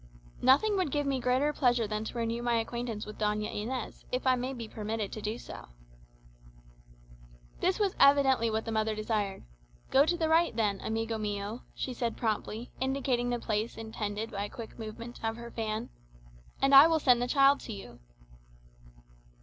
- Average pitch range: Yes, average, 3.4 semitones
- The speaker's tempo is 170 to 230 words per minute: Yes, average, 180 wpm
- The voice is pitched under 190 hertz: No, high, 235 Hz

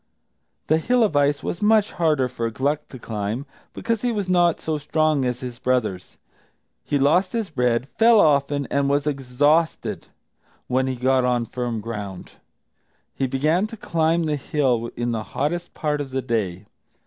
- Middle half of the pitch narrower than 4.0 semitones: No, average, 4.5 semitones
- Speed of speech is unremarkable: Yes, average, 170 wpm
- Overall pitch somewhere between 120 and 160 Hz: Yes, medium, 140 Hz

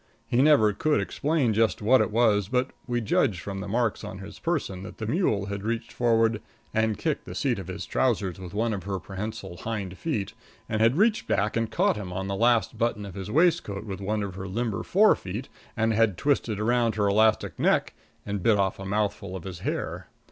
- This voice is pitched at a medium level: No, low, 110 Hz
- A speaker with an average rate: No, fast, 215 wpm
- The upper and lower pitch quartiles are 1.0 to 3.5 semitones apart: Yes, average, 3.2 semitones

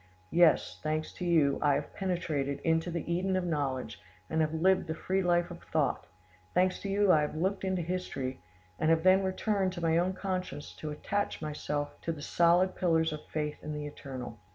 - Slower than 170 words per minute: No, average, 200 wpm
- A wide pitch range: No, average, 3.5 semitones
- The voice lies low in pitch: No, medium, 165 Hz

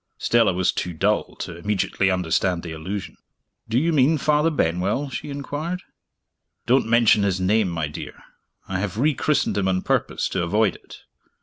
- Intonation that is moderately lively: No, wide, 6.9 semitones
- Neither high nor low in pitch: No, low, 100 Hz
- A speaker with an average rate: Yes, average, 170 wpm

